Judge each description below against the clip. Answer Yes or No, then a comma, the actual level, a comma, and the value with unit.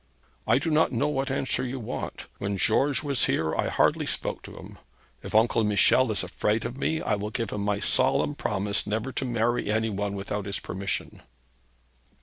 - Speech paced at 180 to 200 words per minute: Yes, average, 190 wpm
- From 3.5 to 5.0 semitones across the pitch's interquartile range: Yes, average, 4.5 semitones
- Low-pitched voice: Yes, low, 110 Hz